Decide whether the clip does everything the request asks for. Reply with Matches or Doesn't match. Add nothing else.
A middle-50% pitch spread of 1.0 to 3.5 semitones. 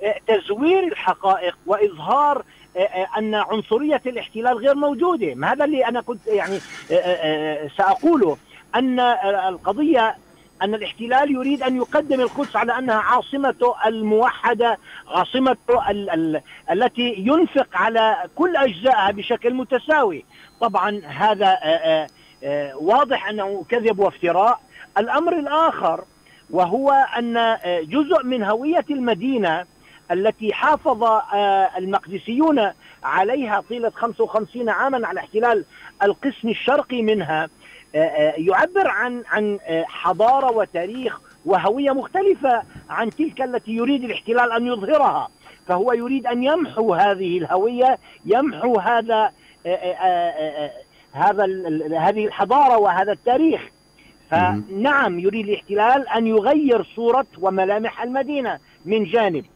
Doesn't match